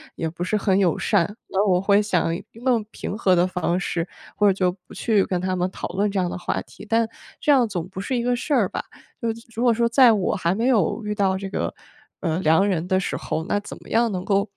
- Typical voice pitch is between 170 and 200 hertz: Yes, high, 195 Hz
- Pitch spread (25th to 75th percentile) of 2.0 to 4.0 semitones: Yes, average, 3.7 semitones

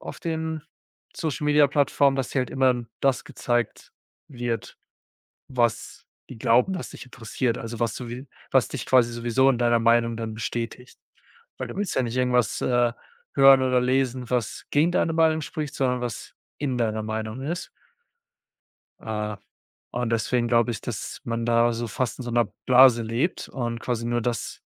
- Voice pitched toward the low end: Yes, low, 120 Hz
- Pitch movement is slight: Yes, narrow, 2.3 semitones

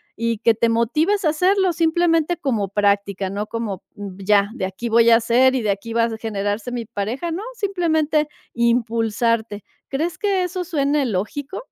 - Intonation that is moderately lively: No, wide, 7.1 semitones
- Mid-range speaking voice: No, high, 235 Hz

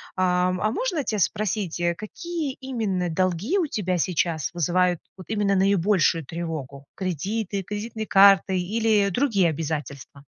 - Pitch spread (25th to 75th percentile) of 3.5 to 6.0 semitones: Yes, average, 3.8 semitones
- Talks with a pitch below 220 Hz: Yes, high, 190 Hz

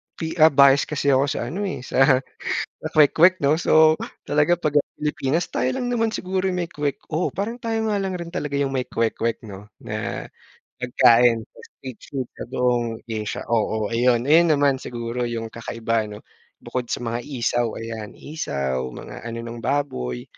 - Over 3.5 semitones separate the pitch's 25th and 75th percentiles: Yes, average, 5.1 semitones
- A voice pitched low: Yes, low, 130 Hz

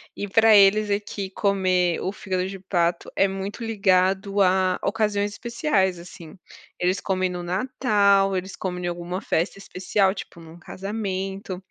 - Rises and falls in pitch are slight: Yes, narrow, 1.7 semitones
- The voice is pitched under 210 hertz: Yes, high, 190 Hz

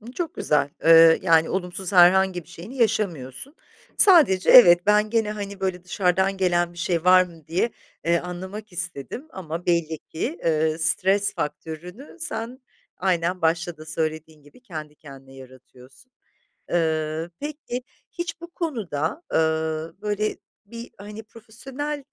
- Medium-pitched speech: Yes, medium, 180 Hz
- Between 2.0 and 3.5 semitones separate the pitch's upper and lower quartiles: No, average, 4.9 semitones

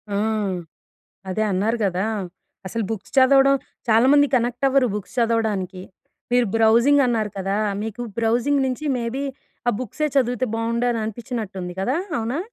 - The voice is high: Yes, high, 230 Hz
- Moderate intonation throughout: Yes, average, 3.0 semitones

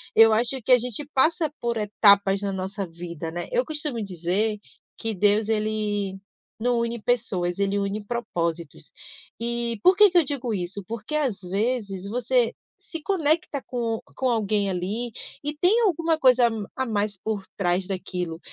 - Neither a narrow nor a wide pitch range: Yes, average, 4.2 semitones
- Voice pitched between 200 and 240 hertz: Yes, high, 220 Hz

